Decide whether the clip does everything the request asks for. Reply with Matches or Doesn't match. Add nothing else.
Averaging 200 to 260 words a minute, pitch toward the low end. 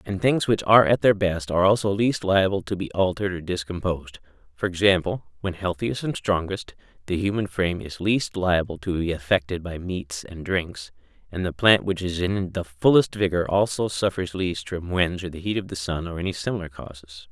Matches